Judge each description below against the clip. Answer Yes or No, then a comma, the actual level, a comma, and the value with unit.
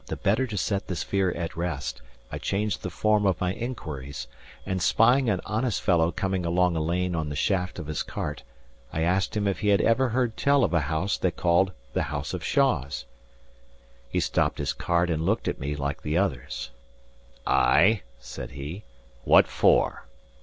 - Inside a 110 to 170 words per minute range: No, average, 190 wpm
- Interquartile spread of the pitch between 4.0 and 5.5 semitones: Yes, average, 4.7 semitones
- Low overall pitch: Yes, very low, 90 Hz